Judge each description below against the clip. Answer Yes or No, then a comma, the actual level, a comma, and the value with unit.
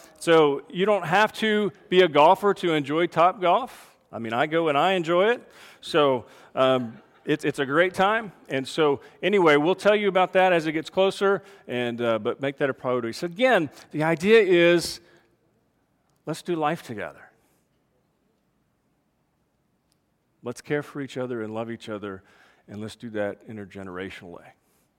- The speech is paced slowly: No, average, 165 wpm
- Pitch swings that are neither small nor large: No, wide, 6.9 semitones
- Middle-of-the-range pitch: Yes, medium, 155 Hz